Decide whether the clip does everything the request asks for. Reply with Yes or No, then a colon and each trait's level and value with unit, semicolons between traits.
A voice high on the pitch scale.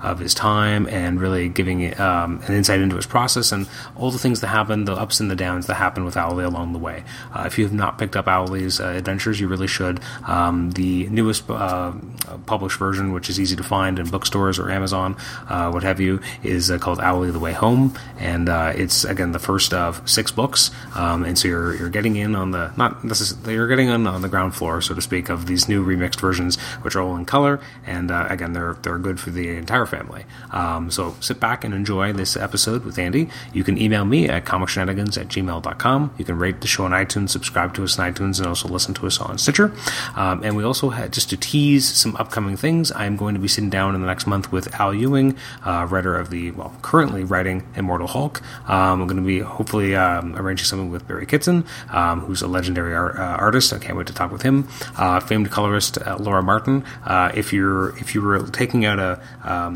No: very low, 95 Hz